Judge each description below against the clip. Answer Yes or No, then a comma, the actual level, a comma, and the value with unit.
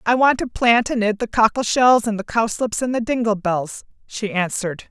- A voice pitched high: Yes, high, 225 Hz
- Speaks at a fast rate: Yes, fast, 220 wpm